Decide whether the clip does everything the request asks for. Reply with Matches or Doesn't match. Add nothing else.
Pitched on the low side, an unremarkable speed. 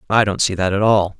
Doesn't match